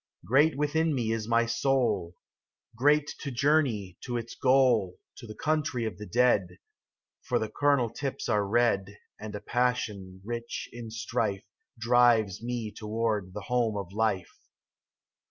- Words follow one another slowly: No, average, 145 wpm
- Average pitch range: Yes, average, 3.2 semitones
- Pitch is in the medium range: No, low, 115 Hz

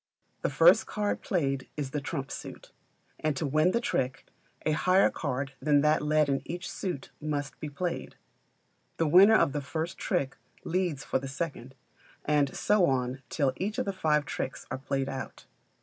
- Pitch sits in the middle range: Yes, medium, 150 Hz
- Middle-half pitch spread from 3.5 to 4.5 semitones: Yes, average, 4.2 semitones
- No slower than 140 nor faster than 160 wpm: No, average, 180 wpm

